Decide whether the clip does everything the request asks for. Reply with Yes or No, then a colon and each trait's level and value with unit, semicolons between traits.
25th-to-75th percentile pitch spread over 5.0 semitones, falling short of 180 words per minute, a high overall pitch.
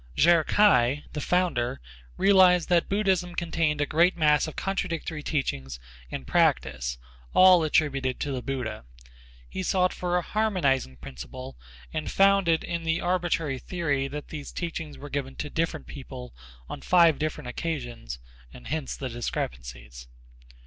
No: wide, 5.4 semitones; average, 145 wpm; medium, 150 Hz